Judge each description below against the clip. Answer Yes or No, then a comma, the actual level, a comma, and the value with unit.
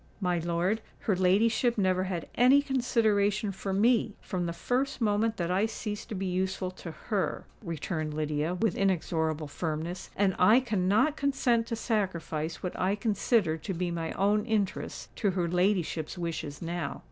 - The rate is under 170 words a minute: Yes, average, 160 wpm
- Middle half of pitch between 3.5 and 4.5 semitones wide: Yes, average, 4.2 semitones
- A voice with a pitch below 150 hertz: No, high, 190 Hz